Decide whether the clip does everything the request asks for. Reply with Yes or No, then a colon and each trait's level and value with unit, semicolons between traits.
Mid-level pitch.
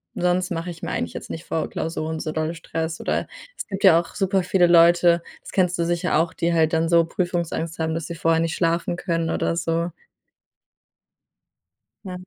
Yes: medium, 170 Hz